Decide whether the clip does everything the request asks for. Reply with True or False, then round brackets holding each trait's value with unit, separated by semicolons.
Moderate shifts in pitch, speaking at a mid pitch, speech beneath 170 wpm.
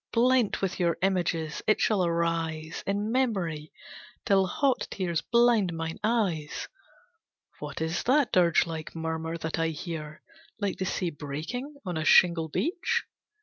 True (4.9 semitones; 175 Hz; 145 wpm)